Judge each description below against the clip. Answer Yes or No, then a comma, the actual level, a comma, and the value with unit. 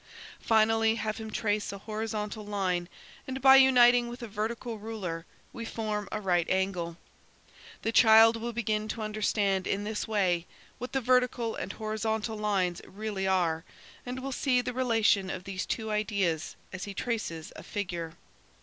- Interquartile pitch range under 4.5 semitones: Yes, average, 2.9 semitones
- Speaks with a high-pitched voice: Yes, high, 215 Hz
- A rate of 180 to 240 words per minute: No, average, 165 wpm